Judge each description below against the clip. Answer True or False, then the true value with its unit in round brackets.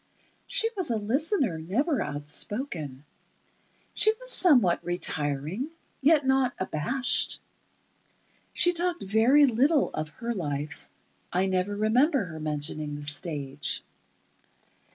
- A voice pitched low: False (205 Hz)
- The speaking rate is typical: False (110 wpm)